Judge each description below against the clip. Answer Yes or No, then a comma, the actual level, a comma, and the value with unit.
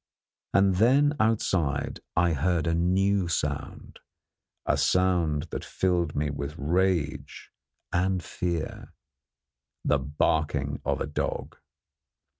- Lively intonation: No, average, 4.1 semitones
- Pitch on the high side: No, very low, 85 Hz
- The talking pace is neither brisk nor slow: No, slow, 105 wpm